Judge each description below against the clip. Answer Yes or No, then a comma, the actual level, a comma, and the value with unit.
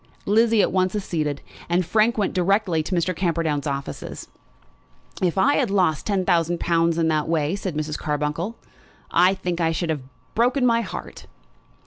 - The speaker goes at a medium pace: Yes, average, 165 wpm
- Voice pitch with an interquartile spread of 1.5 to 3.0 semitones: No, average, 3.7 semitones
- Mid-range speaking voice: Yes, medium, 175 Hz